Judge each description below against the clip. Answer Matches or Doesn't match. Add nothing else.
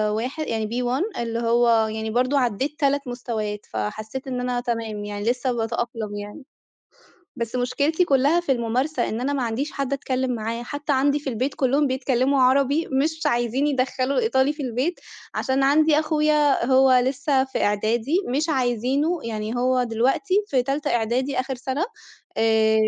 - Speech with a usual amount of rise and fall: Matches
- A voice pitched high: Matches